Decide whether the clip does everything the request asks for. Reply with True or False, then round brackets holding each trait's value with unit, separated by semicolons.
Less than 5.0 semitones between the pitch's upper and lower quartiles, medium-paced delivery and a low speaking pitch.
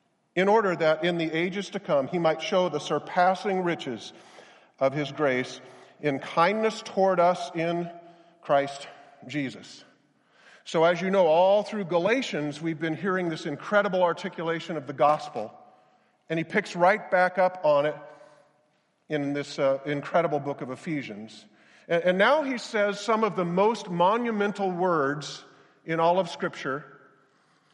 False (4.1 semitones; 150 wpm; 170 Hz)